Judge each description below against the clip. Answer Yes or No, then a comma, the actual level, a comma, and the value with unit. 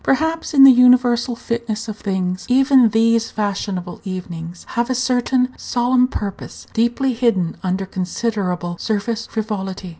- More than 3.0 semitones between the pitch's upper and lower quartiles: Yes, average, 4.6 semitones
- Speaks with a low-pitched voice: No, high, 225 Hz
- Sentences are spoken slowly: Yes, slow, 130 wpm